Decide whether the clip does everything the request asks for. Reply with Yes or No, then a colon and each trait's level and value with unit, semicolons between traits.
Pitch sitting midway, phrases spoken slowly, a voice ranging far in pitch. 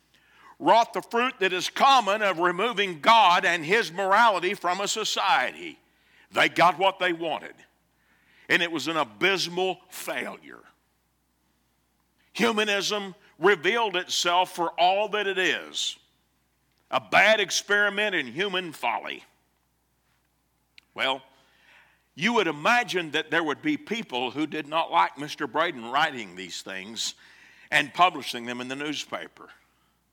Yes: medium, 180 Hz; slow, 125 wpm; wide, 6.9 semitones